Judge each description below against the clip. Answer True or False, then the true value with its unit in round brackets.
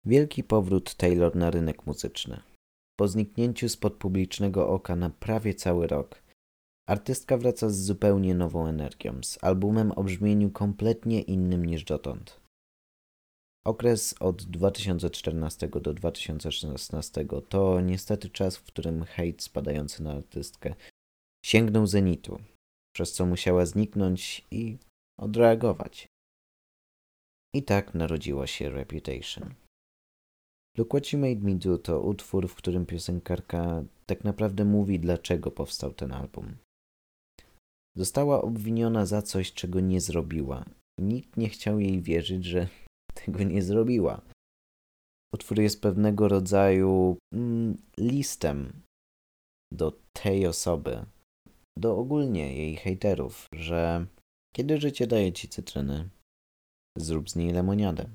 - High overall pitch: False (95 Hz)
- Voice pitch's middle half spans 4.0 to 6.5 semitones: True (4.5 semitones)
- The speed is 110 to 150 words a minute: True (115 wpm)